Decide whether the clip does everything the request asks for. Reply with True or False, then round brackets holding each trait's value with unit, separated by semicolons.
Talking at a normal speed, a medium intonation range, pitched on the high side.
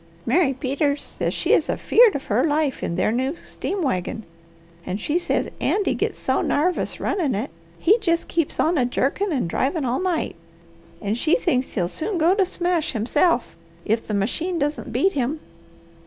False (180 wpm; 6.0 semitones; 295 Hz)